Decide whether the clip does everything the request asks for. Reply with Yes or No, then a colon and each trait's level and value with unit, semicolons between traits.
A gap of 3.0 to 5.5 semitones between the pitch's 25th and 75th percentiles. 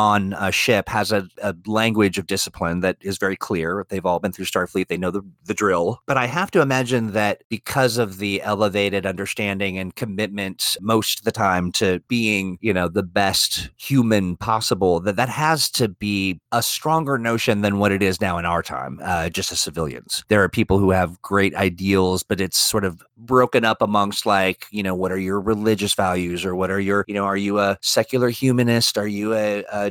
No: narrow, 2.5 semitones